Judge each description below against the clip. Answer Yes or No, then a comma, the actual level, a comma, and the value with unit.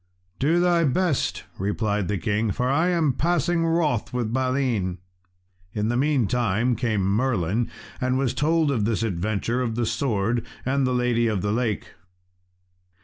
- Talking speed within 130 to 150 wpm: Yes, average, 145 wpm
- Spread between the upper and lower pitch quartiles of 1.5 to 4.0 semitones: No, average, 4.5 semitones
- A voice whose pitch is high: No, low, 120 Hz